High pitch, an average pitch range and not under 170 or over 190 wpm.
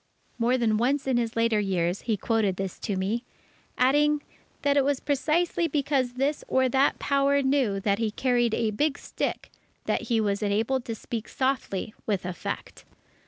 Yes: high, 240 Hz; average, 4.6 semitones; average, 175 wpm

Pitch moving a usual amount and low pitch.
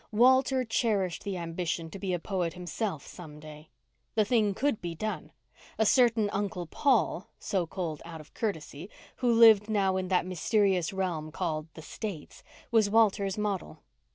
No: average, 4.3 semitones; high, 190 Hz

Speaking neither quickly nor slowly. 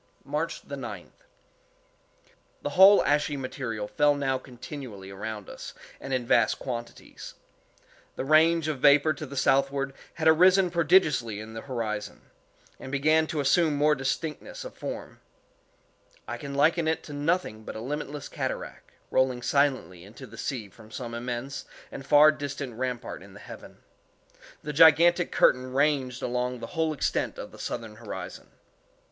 Yes: average, 150 wpm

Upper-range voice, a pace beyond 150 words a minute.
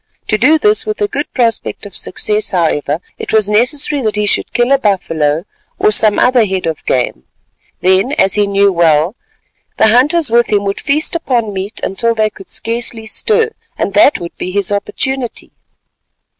Yes: high, 215 Hz; average, 180 wpm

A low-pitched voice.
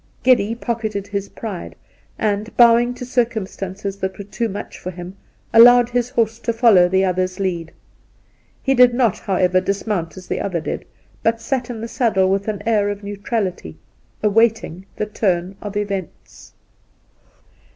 No: high, 205 Hz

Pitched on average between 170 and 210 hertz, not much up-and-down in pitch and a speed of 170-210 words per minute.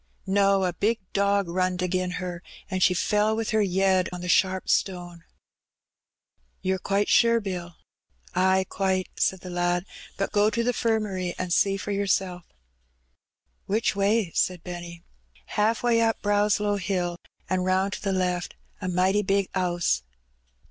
No: high, 190 Hz; narrow, 2.2 semitones; average, 155 wpm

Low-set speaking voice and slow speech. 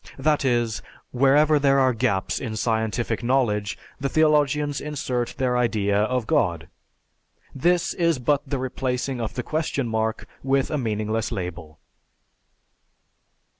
Yes: low, 125 Hz; slow, 130 wpm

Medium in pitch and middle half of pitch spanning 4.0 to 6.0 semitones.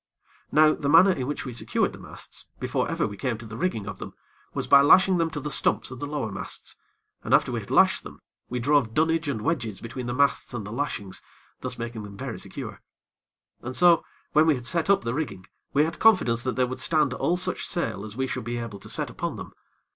No: low, 130 Hz; average, 5.1 semitones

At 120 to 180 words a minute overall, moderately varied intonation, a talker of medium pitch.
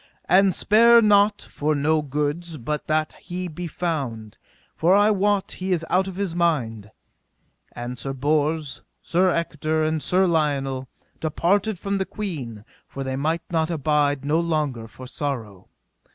Yes: average, 150 wpm; average, 4.5 semitones; medium, 155 Hz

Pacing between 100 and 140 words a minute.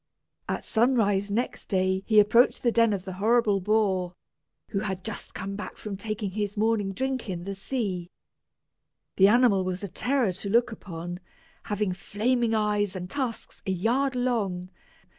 No: average, 160 wpm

